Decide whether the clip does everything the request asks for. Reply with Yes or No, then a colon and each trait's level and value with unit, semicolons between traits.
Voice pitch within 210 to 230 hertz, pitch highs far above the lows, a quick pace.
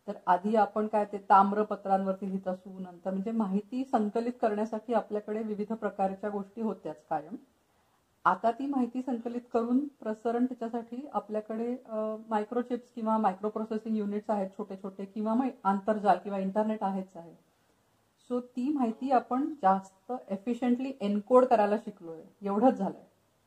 No: high, 215 Hz; average, 3.3 semitones; fast, 135 wpm